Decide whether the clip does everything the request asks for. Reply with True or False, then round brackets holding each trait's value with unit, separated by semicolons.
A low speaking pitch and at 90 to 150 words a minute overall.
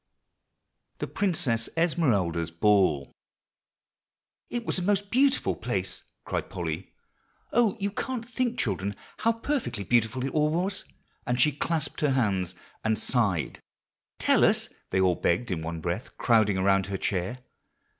True (120 Hz; 140 wpm)